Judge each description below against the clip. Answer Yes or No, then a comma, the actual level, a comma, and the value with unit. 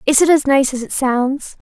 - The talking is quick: Yes, fast, 245 wpm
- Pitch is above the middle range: Yes, very high, 270 Hz